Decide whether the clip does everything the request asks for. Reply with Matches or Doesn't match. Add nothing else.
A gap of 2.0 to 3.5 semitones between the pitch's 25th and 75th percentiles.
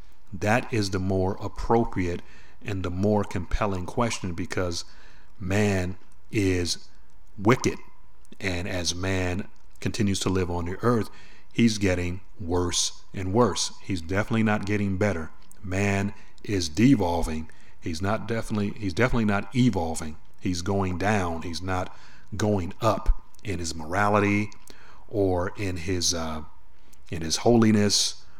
Matches